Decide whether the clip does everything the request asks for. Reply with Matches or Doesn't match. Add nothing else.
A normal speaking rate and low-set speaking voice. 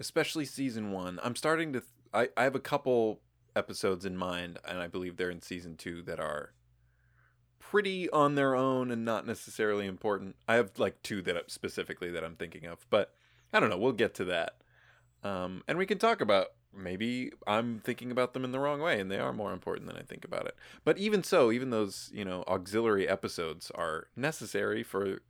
Doesn't match